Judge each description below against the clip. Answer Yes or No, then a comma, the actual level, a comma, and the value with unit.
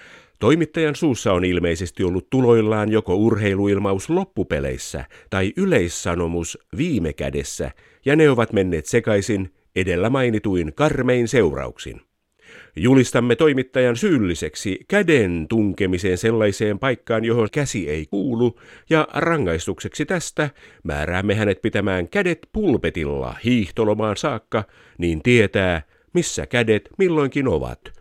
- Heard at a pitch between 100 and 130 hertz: Yes, low, 110 Hz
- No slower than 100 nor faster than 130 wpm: Yes, average, 105 wpm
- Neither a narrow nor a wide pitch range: No, wide, 6.2 semitones